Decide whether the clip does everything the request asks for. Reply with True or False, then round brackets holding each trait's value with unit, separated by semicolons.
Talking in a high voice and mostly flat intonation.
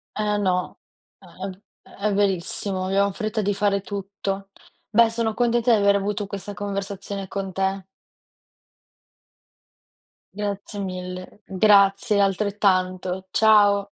True (200 Hz; 1.3 semitones)